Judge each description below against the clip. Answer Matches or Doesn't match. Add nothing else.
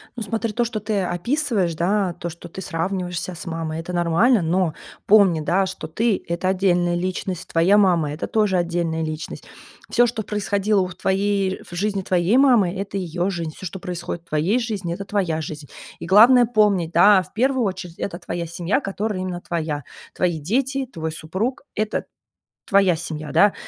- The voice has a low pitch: Doesn't match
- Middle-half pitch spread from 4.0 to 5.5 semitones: Doesn't match